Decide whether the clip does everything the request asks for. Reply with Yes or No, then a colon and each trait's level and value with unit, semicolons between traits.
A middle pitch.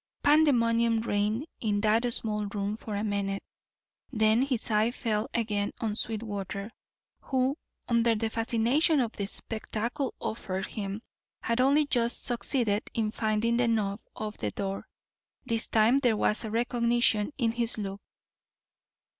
No: high, 225 Hz